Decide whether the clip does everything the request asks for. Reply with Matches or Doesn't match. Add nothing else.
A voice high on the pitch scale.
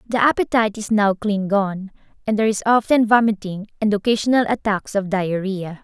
Matches